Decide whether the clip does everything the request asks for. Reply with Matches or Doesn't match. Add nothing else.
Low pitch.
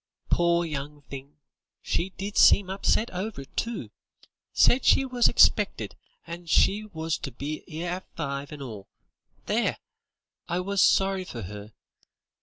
Doesn't match